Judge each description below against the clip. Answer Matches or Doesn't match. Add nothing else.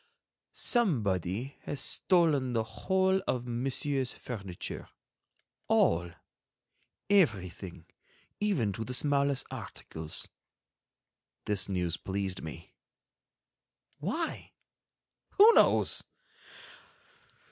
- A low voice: Matches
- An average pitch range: Doesn't match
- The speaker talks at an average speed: Doesn't match